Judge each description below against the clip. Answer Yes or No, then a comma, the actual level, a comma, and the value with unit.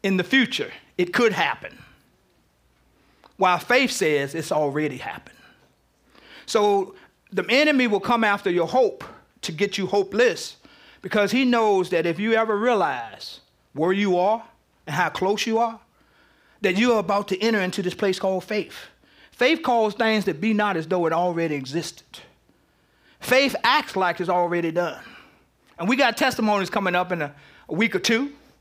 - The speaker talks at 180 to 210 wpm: No, average, 170 wpm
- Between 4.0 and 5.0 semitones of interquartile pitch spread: Yes, average, 4.5 semitones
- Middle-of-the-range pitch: No, high, 200 Hz